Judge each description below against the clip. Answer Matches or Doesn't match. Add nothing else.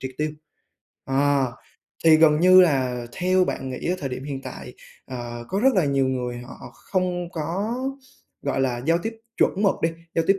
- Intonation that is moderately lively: Doesn't match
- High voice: Doesn't match